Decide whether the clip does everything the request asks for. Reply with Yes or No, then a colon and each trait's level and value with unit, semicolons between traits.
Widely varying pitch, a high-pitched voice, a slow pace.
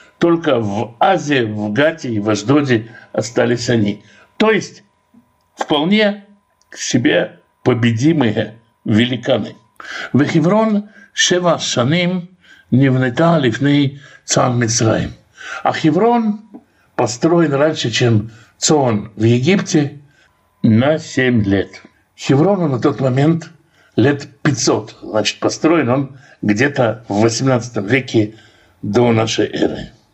No: wide, 6.1 semitones; low, 135 Hz; slow, 105 wpm